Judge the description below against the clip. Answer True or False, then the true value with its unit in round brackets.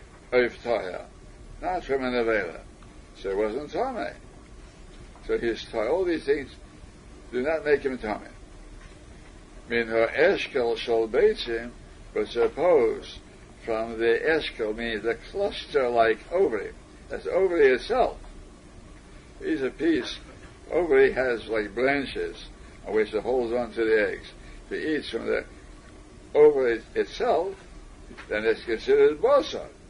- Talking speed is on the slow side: True (130 wpm)